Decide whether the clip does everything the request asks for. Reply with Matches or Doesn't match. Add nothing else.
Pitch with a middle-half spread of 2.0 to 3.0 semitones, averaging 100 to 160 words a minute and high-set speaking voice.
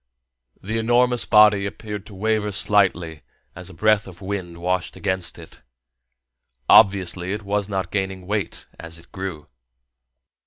Doesn't match